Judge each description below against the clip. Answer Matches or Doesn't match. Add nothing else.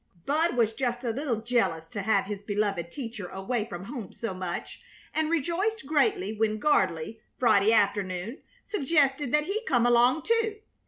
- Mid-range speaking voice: Doesn't match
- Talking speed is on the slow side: Doesn't match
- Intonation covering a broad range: Matches